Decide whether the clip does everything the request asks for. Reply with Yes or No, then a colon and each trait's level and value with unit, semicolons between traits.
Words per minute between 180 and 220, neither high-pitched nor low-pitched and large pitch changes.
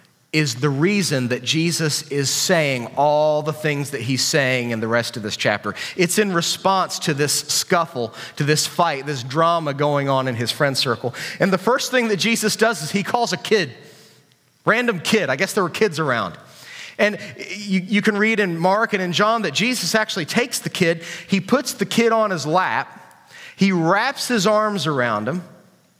Yes: average, 195 wpm; medium, 170 Hz; wide, 6.1 semitones